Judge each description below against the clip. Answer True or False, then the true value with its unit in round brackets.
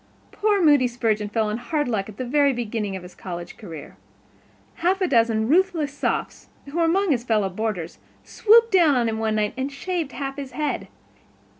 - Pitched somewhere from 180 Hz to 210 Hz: False (250 Hz)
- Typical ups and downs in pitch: False (6.3 semitones)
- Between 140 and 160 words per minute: False (195 wpm)